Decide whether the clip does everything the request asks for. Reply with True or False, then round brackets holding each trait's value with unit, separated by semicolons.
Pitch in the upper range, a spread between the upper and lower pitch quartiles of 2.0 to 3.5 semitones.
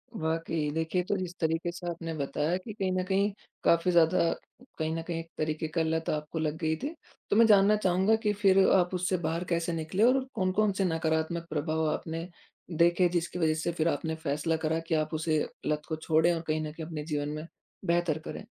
False (165 Hz; 2.4 semitones)